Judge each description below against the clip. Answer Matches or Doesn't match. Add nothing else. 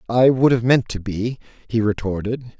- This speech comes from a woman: Doesn't match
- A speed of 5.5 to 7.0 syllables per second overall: Doesn't match